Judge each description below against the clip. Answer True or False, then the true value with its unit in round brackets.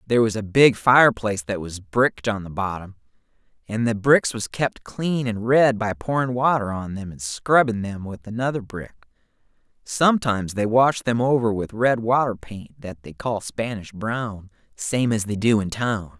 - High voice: False (110 Hz)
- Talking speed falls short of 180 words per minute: False (185 wpm)